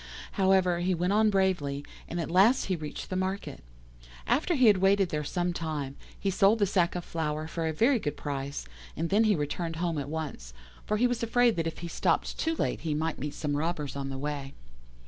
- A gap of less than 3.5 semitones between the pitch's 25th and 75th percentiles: No, average, 4.7 semitones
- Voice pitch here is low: No, medium, 170 Hz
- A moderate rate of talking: No, fast, 220 wpm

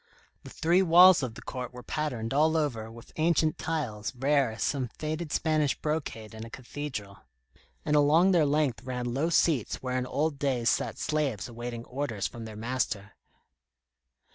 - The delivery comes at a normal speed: Yes, average, 165 wpm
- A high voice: No, low, 135 Hz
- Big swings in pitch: No, average, 4.7 semitones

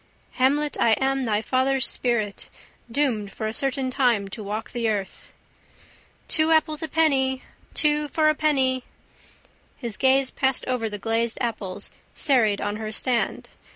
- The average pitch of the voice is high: Yes, very high, 255 Hz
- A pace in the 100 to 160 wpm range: Yes, average, 150 wpm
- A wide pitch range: No, average, 3.8 semitones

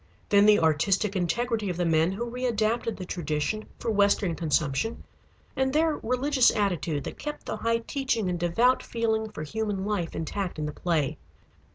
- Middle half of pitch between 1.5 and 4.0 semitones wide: No, average, 5.3 semitones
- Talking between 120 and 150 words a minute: No, average, 170 wpm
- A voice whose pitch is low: No, high, 205 Hz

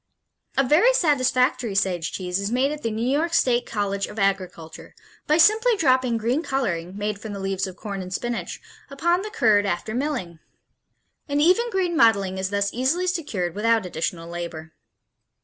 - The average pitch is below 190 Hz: No, high, 225 Hz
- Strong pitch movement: Yes, wide, 7.2 semitones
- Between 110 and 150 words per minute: No, average, 170 wpm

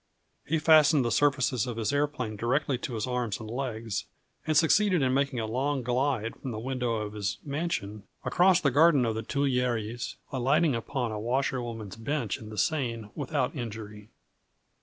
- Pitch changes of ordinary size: Yes, average, 4.2 semitones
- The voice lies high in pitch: No, low, 125 Hz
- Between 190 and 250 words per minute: No, average, 170 wpm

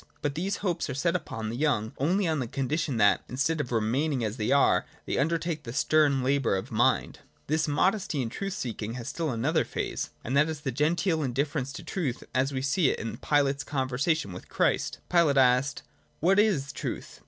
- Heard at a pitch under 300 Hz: Yes, medium, 140 Hz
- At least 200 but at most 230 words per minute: Yes, fast, 205 wpm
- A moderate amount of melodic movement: Yes, average, 4.0 semitones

